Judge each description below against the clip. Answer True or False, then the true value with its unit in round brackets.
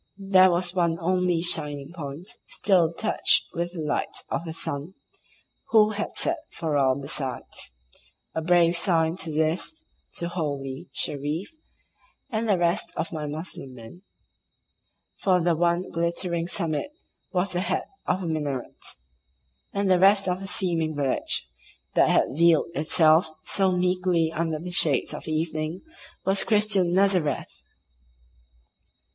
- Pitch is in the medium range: True (170 Hz)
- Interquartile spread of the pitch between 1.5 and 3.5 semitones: True (3.0 semitones)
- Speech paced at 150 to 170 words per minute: False (135 wpm)